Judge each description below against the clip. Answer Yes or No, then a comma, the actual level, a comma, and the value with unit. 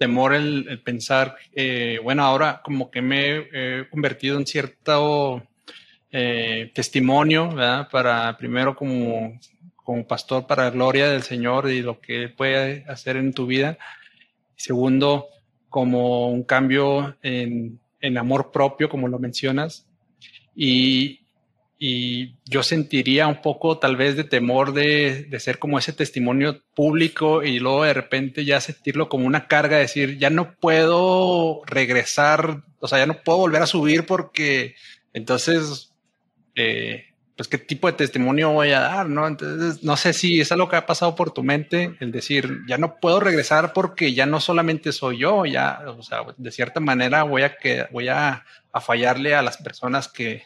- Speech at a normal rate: Yes, average, 165 wpm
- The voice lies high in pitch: No, medium, 140 Hz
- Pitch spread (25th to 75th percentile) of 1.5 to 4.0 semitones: Yes, average, 3.1 semitones